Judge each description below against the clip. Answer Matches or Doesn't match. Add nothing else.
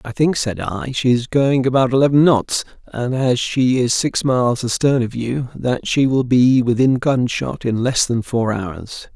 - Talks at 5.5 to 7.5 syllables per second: Doesn't match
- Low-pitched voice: Matches